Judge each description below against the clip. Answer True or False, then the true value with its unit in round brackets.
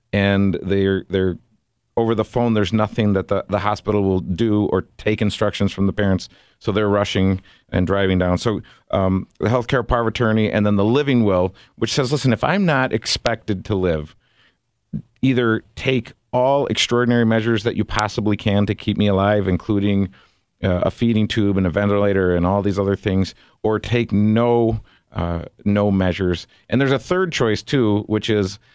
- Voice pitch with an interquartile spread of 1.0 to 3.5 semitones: True (3.0 semitones)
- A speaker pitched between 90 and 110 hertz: True (105 Hz)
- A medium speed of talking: True (180 wpm)